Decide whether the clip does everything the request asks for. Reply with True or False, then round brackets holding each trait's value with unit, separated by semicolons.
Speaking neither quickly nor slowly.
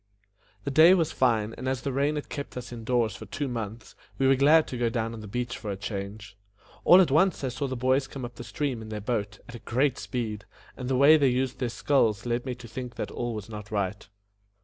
False (255 wpm)